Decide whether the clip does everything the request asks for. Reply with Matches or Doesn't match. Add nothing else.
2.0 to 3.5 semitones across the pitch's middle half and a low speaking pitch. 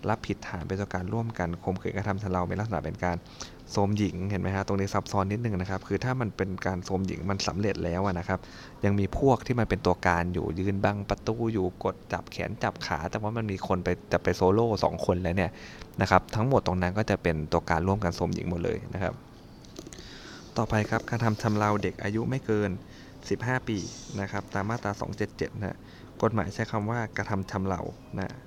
Matches